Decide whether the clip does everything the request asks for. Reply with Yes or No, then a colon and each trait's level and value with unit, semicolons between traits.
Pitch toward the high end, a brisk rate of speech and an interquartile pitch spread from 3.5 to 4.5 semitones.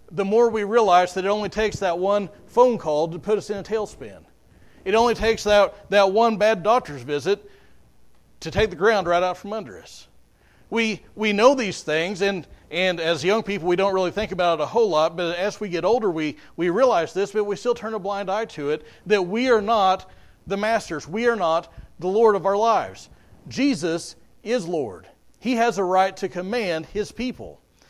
Yes: high, 200 Hz; fast, 210 wpm; average, 4.1 semitones